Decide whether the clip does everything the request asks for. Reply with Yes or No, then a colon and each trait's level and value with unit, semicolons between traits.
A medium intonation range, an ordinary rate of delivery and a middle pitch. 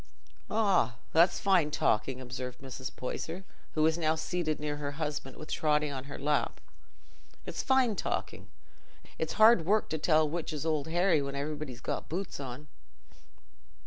Yes: average, 3.4 semitones; average, 155 wpm; medium, 155 Hz